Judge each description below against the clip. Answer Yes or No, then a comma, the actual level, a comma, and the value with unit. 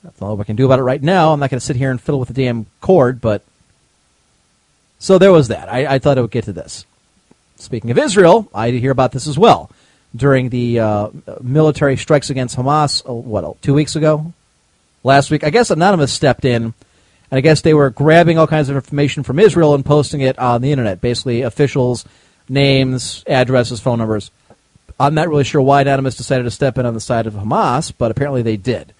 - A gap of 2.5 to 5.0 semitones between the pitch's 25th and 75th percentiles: Yes, average, 3.4 semitones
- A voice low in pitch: Yes, low, 130 Hz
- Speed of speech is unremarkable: No, fast, 220 wpm